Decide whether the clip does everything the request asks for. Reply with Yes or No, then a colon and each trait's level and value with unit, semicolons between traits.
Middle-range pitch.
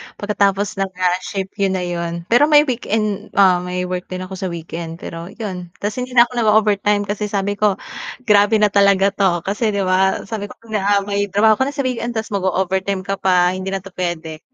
No: high, 195 Hz